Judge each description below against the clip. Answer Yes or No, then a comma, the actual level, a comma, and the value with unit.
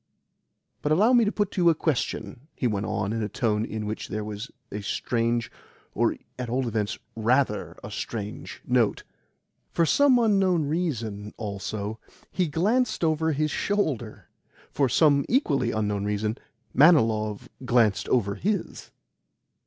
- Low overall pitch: Yes, low, 120 Hz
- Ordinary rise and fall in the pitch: No, wide, 7.1 semitones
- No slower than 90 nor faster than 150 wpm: Yes, average, 145 wpm